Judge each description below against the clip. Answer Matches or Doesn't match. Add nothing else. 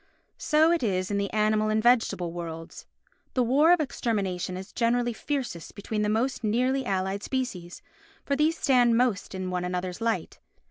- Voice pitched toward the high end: Matches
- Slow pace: Doesn't match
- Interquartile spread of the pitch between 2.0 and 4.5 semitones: Doesn't match